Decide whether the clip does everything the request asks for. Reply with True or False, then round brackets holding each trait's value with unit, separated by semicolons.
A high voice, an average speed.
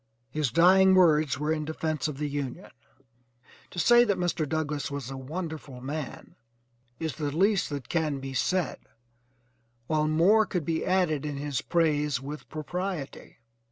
False (155 Hz; 155 wpm)